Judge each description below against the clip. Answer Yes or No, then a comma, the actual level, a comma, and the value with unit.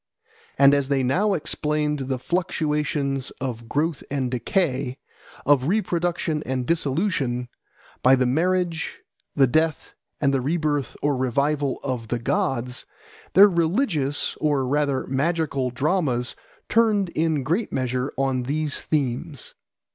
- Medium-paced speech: No, slow, 125 wpm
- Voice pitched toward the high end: No, medium, 145 Hz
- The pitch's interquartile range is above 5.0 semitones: No, average, 4.0 semitones